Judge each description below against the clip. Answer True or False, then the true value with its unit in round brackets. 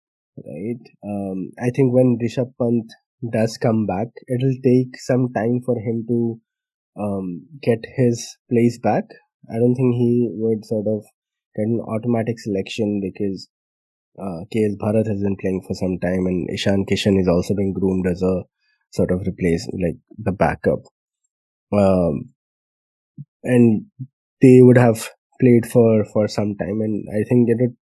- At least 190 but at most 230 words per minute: False (160 wpm)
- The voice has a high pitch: False (110 Hz)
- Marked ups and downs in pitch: False (3.6 semitones)